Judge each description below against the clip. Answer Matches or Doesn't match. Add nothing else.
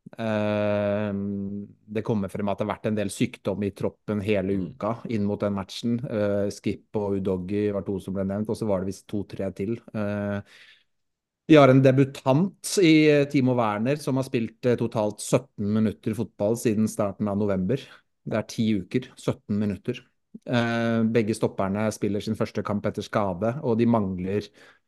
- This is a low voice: Matches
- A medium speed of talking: Matches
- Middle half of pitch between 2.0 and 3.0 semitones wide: Matches